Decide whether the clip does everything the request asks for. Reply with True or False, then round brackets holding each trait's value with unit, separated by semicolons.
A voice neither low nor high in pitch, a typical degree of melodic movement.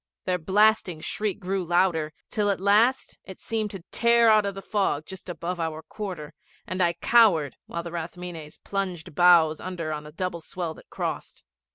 True (180 Hz; 3.5 semitones)